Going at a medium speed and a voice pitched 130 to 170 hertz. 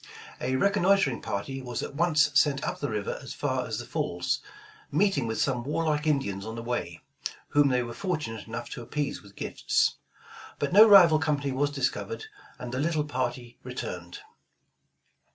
Yes: average, 170 wpm; medium, 140 Hz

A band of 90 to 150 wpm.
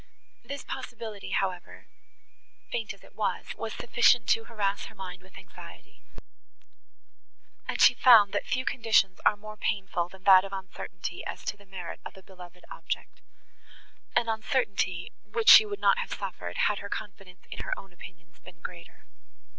No: average, 160 wpm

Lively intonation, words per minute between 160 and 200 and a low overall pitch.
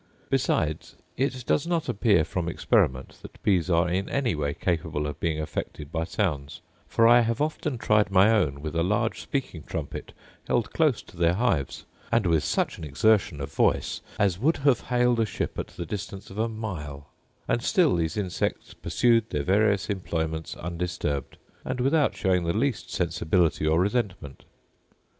Yes: wide, 6.4 semitones; average, 170 wpm; very low, 95 Hz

